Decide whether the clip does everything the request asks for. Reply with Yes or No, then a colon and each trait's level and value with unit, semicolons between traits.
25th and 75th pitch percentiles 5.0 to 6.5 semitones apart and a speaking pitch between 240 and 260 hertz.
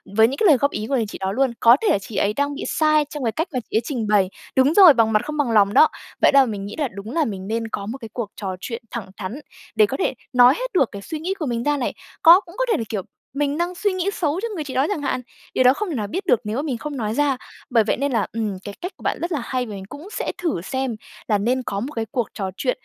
Yes: wide, 5.6 semitones; very high, 255 Hz